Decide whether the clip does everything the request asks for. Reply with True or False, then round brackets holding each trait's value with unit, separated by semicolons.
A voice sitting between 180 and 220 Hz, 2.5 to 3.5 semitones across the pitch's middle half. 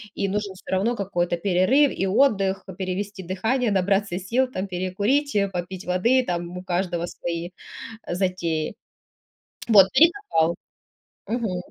True (190 Hz; 2.9 semitones)